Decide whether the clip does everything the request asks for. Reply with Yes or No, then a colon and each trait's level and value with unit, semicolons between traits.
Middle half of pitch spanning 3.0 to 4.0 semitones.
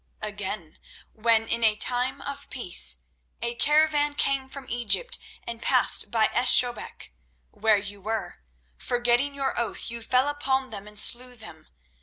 Yes: average, 3.7 semitones